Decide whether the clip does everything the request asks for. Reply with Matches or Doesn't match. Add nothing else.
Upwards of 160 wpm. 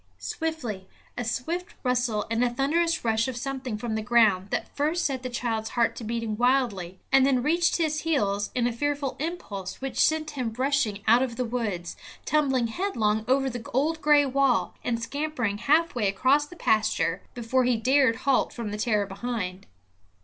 Matches